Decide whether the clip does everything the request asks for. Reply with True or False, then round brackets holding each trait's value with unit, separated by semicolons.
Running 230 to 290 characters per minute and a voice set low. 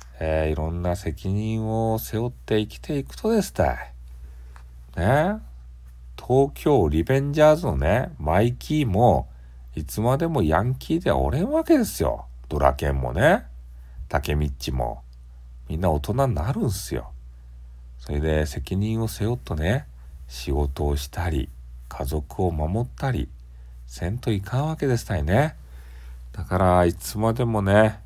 True (270 characters per minute; 80 Hz)